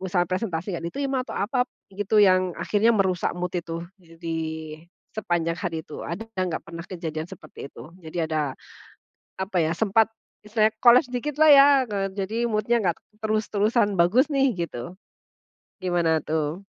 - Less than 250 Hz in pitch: Yes, medium, 185 Hz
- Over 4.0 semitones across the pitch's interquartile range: Yes, average, 4.4 semitones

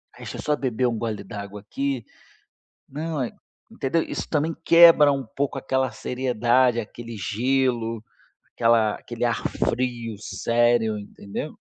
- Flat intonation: No, average, 3.1 semitones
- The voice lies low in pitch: Yes, low, 120 Hz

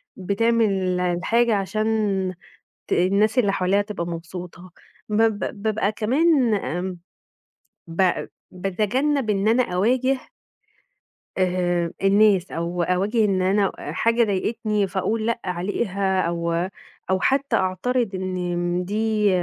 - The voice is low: No, high, 195 Hz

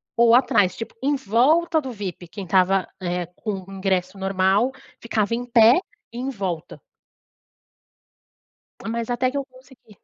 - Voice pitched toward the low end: No, high, 225 Hz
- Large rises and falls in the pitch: No, average, 4.9 semitones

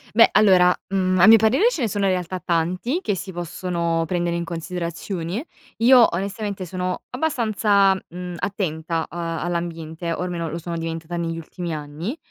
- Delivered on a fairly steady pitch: No, average, 3.0 semitones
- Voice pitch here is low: No, medium, 180 Hz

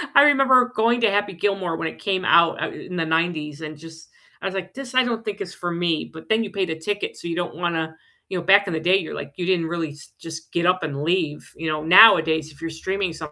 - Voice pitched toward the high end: No, medium, 175 Hz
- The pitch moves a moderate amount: Yes, average, 3.7 semitones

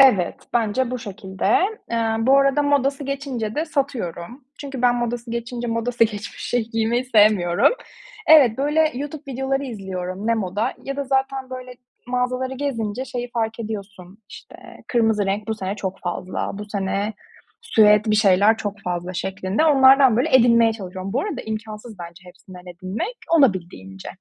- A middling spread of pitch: Yes, average, 4.7 semitones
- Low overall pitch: No, high, 230 Hz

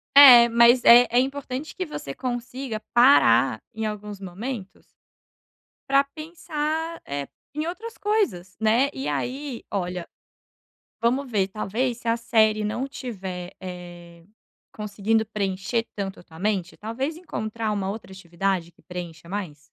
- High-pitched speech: Yes, high, 220 Hz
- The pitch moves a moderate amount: No, wide, 5.7 semitones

